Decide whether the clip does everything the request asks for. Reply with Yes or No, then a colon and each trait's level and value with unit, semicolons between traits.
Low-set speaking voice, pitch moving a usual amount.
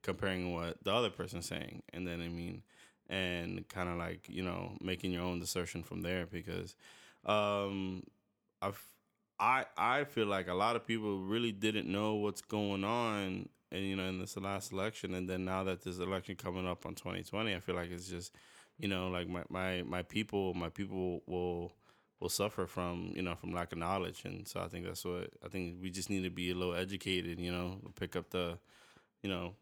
No: very low, 90 Hz; narrow, 1.9 semitones